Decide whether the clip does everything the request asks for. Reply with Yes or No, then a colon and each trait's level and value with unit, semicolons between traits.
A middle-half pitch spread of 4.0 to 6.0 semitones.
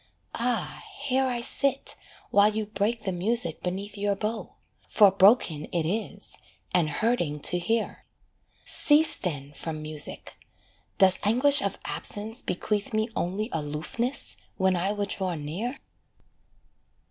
Yes: average, 4.8 semitones